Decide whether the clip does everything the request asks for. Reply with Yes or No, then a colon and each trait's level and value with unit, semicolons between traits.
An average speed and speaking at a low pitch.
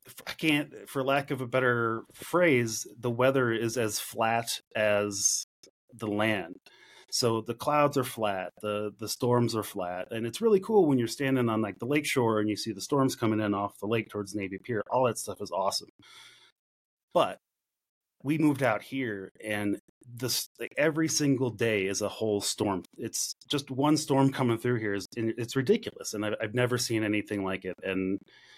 Yes: average, 185 wpm; low, 115 Hz